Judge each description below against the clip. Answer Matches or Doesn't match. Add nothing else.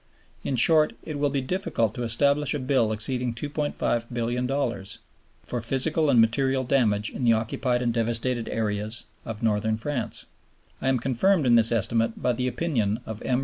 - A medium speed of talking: Matches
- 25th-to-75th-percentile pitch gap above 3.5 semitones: Doesn't match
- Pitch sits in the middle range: Doesn't match